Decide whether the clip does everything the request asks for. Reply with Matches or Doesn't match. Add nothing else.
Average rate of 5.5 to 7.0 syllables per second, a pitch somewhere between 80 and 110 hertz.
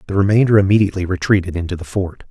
Doesn't match